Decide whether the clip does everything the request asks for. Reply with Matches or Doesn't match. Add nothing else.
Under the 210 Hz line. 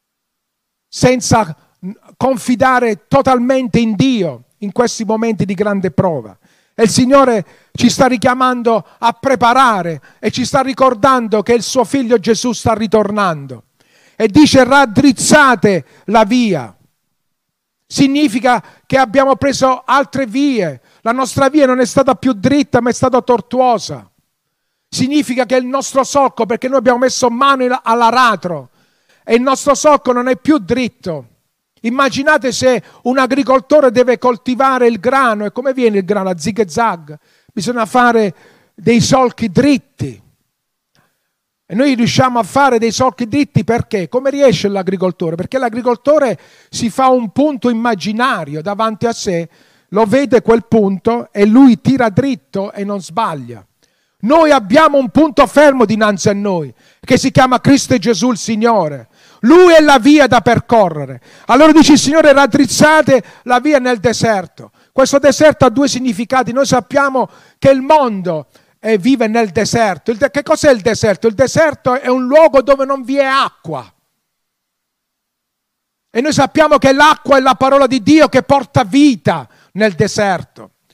Doesn't match